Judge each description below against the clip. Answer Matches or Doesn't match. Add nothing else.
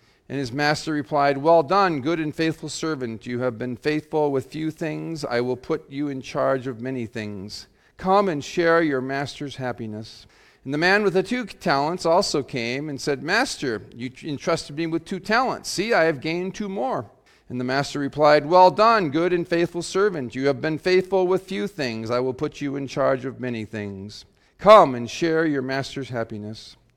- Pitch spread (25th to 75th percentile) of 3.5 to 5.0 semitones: Matches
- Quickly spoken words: Doesn't match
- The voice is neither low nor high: Matches